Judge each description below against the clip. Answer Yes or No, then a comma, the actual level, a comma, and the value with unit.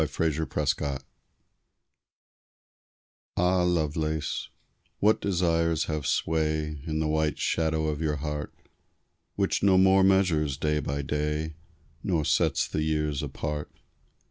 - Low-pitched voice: Yes, very low, 80 Hz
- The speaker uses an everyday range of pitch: No, narrow, 1.7 semitones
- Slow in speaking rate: Yes, slow, 115 wpm